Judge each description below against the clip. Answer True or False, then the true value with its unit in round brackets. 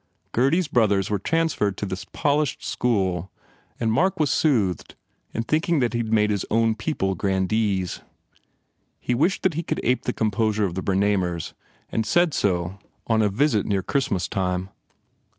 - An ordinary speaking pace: True (170 wpm)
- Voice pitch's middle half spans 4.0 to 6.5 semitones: True (5.5 semitones)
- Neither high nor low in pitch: False (110 Hz)